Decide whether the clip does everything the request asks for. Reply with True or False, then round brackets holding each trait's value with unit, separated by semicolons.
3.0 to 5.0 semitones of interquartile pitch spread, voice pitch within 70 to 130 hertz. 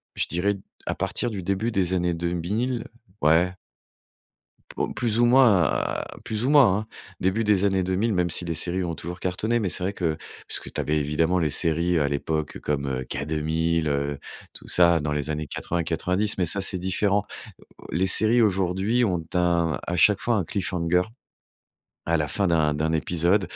True (3.6 semitones; 90 Hz)